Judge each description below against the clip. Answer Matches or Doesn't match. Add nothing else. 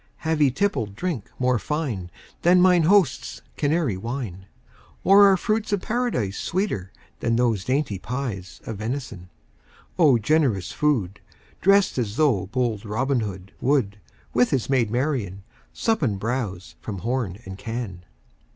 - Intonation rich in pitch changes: Matches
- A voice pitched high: Doesn't match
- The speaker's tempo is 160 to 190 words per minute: Doesn't match